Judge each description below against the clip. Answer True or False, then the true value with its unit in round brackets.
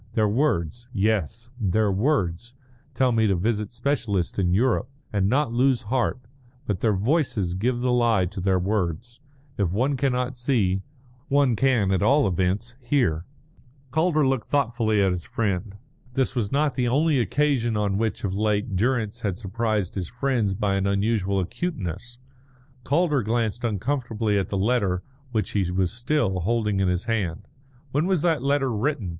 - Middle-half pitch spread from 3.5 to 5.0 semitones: True (4.7 semitones)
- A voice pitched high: False (110 Hz)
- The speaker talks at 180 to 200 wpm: False (160 wpm)